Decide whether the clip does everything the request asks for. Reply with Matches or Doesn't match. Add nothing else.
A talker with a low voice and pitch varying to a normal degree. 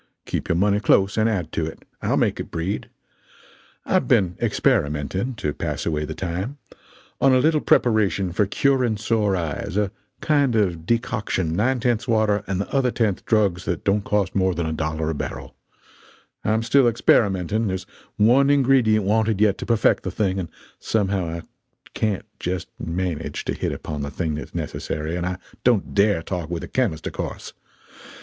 Matches